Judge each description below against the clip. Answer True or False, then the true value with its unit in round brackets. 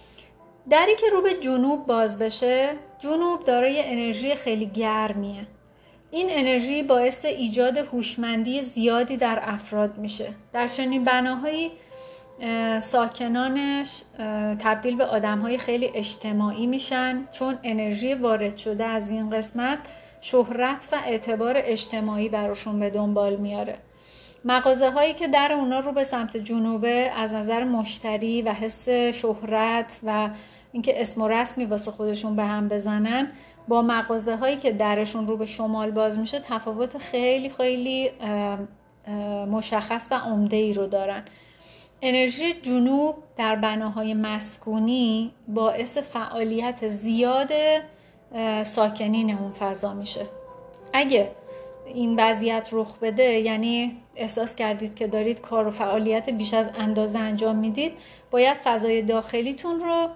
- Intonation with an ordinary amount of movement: True (3.0 semitones)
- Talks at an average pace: True (125 wpm)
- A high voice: True (230 Hz)